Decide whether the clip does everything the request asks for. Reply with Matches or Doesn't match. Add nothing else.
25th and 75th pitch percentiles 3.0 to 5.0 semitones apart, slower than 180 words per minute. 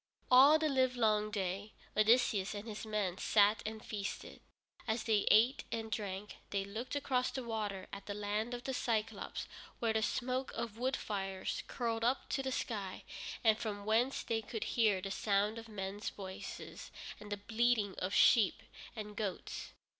Doesn't match